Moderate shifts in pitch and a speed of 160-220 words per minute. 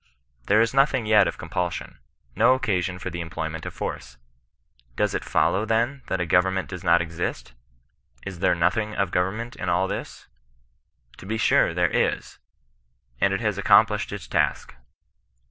Yes: average, 3.7 semitones; average, 175 wpm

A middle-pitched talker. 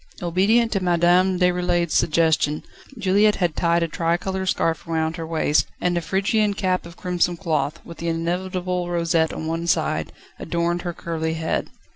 Yes: medium, 175 Hz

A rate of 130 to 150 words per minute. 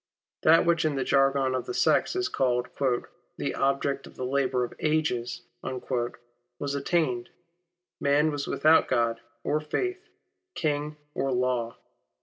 Yes: average, 140 wpm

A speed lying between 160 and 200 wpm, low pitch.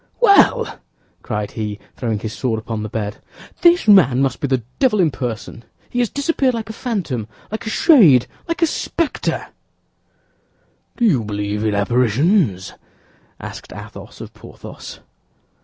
No: average, 145 wpm; low, 130 Hz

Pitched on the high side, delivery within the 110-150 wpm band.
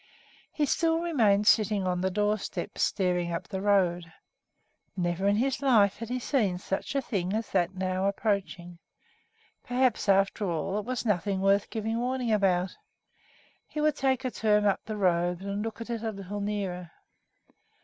No: high, 205 Hz; average, 170 wpm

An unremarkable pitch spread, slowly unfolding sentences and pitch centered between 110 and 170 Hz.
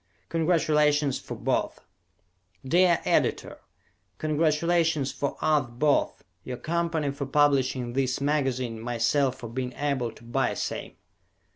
Yes: average, 3.2 semitones; slow, 115 wpm; medium, 140 Hz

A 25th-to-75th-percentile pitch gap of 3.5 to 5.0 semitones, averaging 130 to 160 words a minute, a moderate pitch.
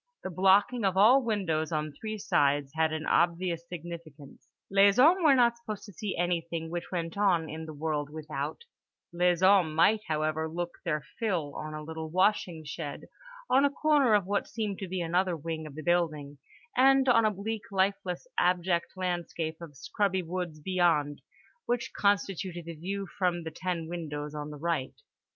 No: average, 4.0 semitones; average, 175 wpm; medium, 175 Hz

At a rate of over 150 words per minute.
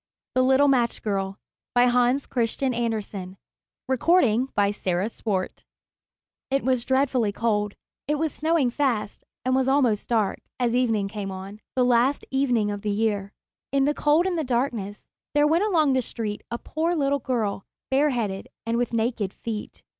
No: average, 145 wpm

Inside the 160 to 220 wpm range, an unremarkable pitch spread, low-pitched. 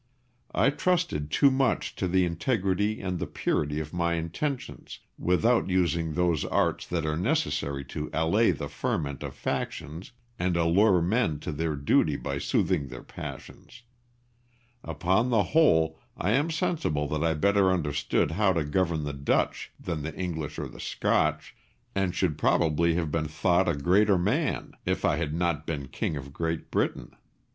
Yes: average, 165 wpm; average, 3.8 semitones; very low, 85 Hz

